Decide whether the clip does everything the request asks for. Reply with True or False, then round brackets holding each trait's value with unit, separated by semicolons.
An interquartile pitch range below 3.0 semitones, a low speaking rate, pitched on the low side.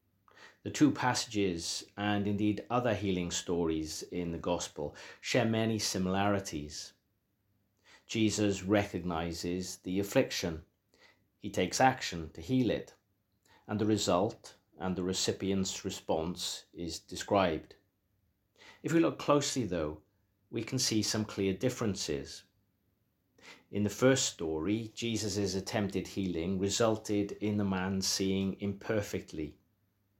True (2.5 semitones; 115 wpm; 100 Hz)